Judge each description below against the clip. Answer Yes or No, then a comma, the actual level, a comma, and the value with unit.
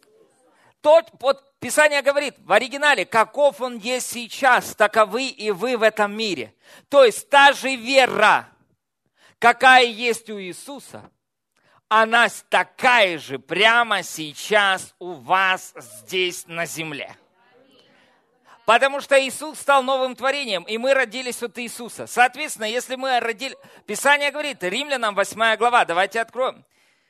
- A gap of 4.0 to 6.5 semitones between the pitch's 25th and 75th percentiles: Yes, average, 4.4 semitones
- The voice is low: No, high, 240 Hz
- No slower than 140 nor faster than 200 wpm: No, average, 125 wpm